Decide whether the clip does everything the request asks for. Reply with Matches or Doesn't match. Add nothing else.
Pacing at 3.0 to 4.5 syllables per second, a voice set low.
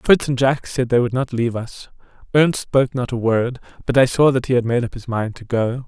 Doesn't match